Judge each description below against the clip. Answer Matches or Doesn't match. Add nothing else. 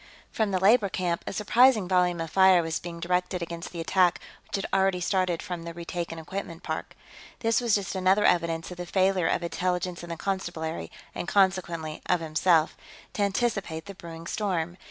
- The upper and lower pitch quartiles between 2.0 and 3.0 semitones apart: Matches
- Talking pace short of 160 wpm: Doesn't match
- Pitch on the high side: Doesn't match